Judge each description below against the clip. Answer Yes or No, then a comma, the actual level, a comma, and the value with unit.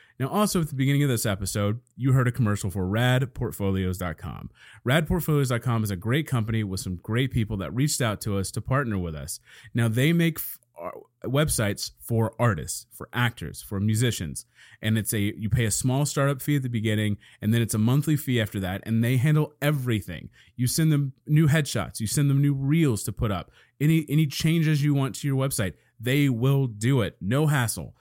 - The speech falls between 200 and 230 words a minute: Yes, fast, 205 wpm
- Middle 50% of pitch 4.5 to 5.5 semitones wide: Yes, average, 5.0 semitones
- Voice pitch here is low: Yes, low, 120 Hz